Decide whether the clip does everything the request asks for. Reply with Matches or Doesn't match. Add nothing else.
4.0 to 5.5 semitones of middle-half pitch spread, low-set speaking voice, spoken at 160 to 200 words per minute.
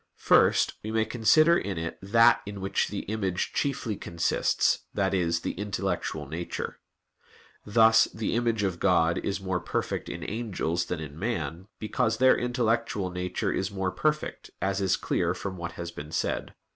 Matches